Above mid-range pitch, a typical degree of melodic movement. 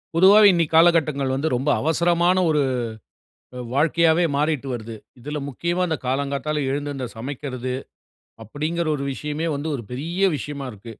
No: medium, 150 Hz; average, 3.5 semitones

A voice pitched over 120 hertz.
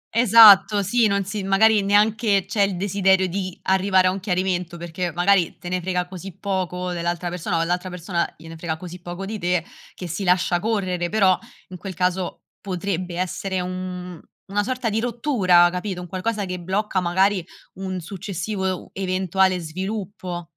Yes: medium, 185 Hz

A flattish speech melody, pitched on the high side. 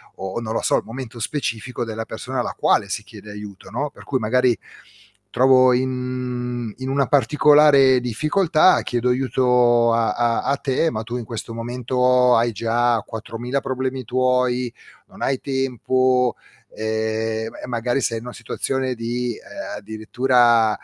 No: narrow, 2.1 semitones; low, 125 Hz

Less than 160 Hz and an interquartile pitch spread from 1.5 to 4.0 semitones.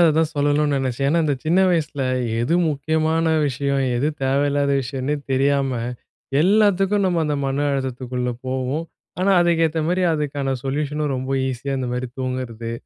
Yes: medium, 140 Hz; average, 3.1 semitones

